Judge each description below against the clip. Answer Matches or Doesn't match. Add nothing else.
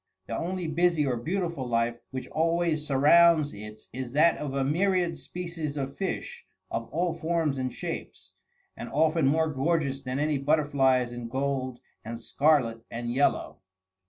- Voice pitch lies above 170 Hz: Doesn't match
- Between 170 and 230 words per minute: Doesn't match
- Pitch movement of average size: Matches